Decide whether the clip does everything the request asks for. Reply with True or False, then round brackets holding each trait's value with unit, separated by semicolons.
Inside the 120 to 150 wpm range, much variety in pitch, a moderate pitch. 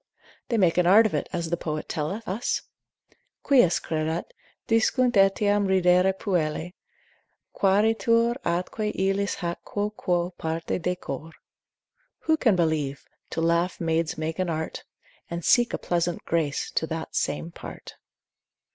False (135 wpm; 3.8 semitones; 180 Hz)